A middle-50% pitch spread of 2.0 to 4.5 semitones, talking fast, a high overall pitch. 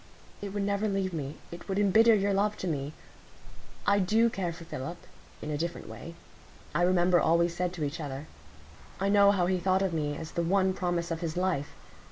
No: average, 2.9 semitones; fast, 210 wpm; medium, 180 Hz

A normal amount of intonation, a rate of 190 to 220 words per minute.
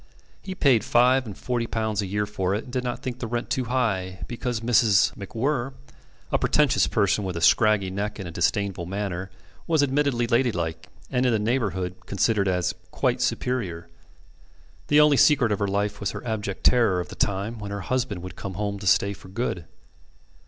Yes: average, 4.2 semitones; average, 195 wpm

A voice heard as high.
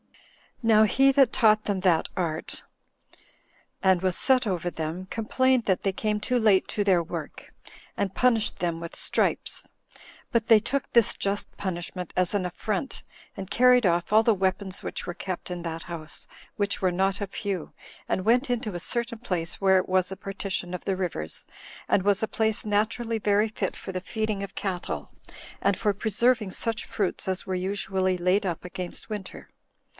Yes: high, 195 Hz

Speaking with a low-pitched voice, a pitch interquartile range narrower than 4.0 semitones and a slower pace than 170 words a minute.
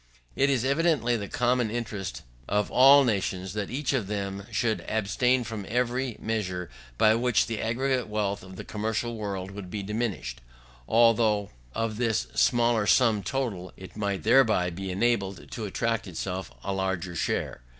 Yes: low, 110 Hz; average, 3.6 semitones; average, 160 wpm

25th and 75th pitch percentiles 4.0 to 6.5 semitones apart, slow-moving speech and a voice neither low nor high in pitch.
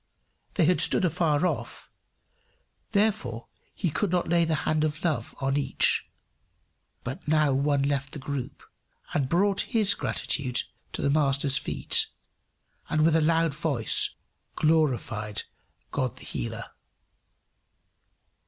No: average, 3.4 semitones; slow, 125 wpm; medium, 150 Hz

